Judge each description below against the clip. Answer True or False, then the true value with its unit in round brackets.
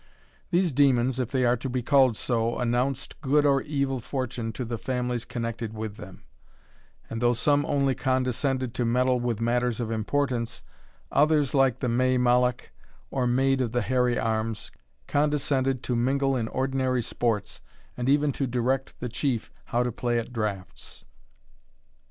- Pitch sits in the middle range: False (125 Hz)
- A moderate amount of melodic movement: False (2.3 semitones)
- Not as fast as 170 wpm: True (160 wpm)